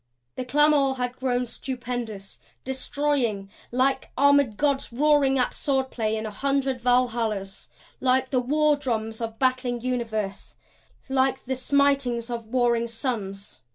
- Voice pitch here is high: Yes, very high, 250 Hz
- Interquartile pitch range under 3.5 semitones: Yes, average, 2.7 semitones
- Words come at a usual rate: No, slow, 130 wpm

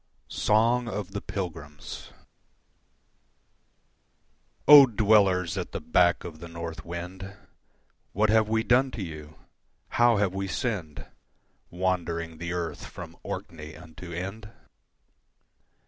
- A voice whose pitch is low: Yes, very low, 90 Hz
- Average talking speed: No, slow, 115 wpm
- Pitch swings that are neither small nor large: Yes, average, 4.2 semitones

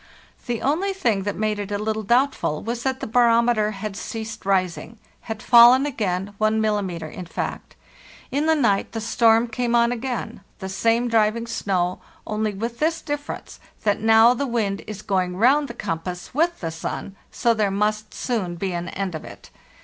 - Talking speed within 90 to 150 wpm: No, average, 175 wpm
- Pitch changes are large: No, average, 3.3 semitones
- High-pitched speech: Yes, high, 220 Hz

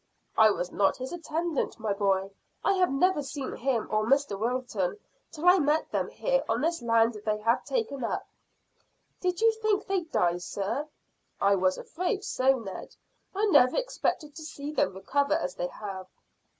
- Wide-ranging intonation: Yes, wide, 8.0 semitones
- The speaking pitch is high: Yes, very high, 265 Hz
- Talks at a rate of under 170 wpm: No, average, 175 wpm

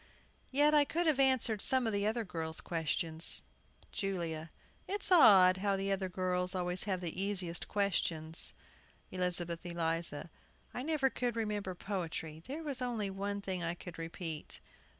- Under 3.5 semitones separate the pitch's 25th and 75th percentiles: No, average, 4.6 semitones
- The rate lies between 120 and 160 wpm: Yes, average, 150 wpm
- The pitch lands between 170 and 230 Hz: Yes, high, 190 Hz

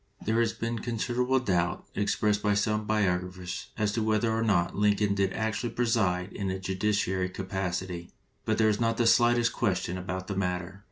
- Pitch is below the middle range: Yes, low, 105 Hz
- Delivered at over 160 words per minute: Yes, average, 175 wpm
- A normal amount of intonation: Yes, average, 3.3 semitones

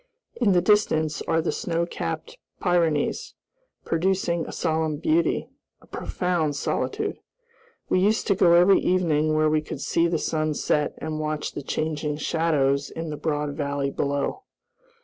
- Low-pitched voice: No, medium, 160 Hz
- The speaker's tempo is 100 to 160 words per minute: Yes, average, 150 wpm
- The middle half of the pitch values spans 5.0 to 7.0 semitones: No, average, 2.8 semitones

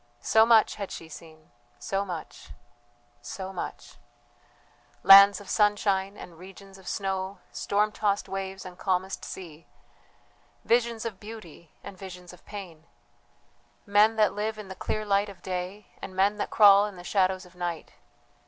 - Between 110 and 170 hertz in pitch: No, high, 195 Hz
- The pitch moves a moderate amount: No, narrow, 2.2 semitones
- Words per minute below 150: No, average, 155 wpm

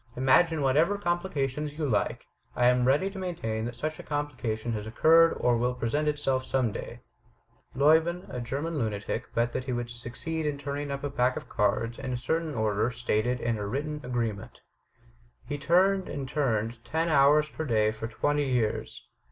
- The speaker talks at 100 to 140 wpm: No, average, 185 wpm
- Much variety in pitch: No, average, 4.4 semitones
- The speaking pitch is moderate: No, low, 130 Hz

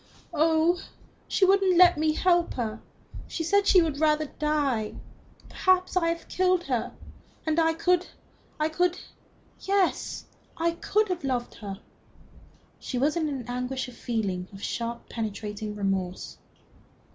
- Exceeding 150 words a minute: No, average, 145 wpm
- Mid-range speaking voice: No, very high, 310 Hz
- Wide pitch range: Yes, wide, 6.9 semitones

